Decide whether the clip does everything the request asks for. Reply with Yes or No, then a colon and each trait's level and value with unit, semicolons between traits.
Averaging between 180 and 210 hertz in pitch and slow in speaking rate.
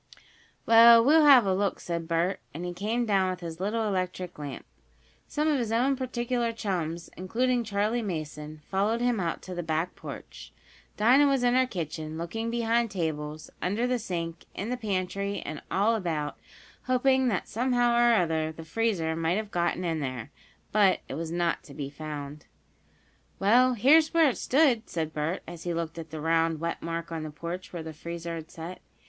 No: medium, 185 Hz; average, 190 wpm